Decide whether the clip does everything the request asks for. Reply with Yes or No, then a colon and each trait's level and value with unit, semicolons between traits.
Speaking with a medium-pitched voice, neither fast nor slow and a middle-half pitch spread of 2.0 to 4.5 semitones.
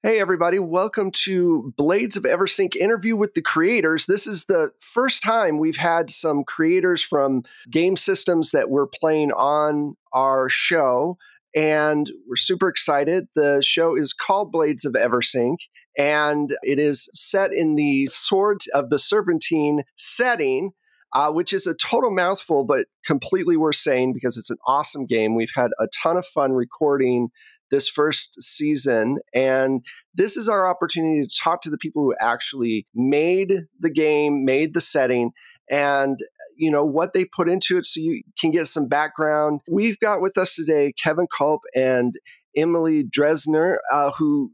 No: medium, 155 Hz; average, 160 wpm; average, 5.1 semitones